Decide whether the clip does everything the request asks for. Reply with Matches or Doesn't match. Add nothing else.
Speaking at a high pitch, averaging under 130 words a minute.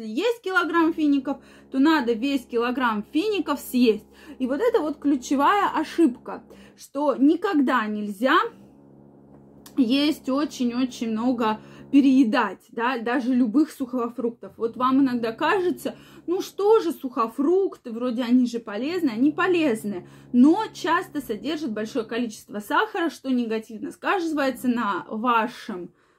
Matches